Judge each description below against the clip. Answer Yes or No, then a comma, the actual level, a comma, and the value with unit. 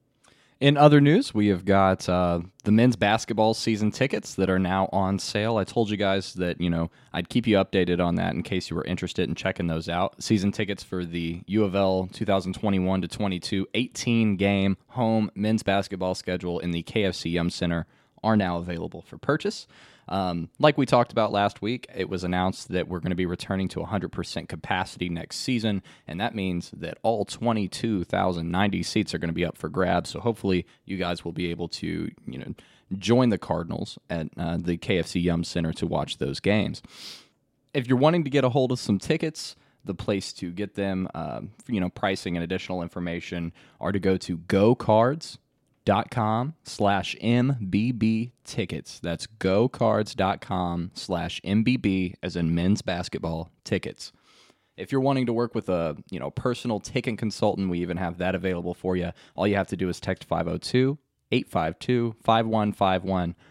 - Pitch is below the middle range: Yes, very low, 95 Hz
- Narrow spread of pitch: No, average, 4.1 semitones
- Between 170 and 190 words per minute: Yes, average, 180 wpm